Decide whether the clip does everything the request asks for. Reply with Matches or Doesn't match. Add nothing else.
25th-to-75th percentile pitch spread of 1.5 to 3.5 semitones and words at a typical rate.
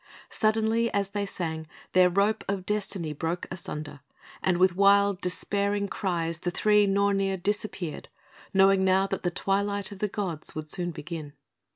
Matches